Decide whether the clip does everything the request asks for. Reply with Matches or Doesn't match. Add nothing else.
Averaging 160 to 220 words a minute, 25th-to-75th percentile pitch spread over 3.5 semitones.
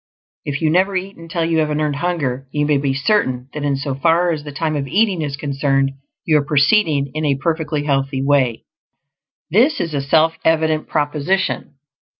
Doesn't match